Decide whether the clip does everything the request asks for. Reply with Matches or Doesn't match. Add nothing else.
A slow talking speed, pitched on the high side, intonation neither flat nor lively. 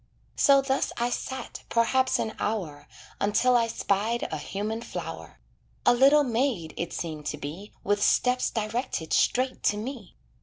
Doesn't match